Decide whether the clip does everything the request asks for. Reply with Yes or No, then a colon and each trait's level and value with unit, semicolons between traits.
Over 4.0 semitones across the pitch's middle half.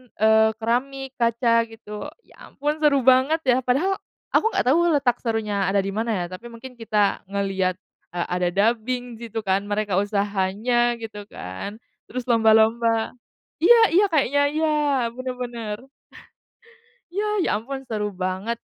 No: average, 3.6 semitones